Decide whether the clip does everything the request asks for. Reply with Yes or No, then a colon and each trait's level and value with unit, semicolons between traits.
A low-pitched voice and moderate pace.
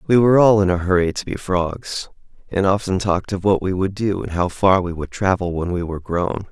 No: very low, 95 Hz; fast, 250 wpm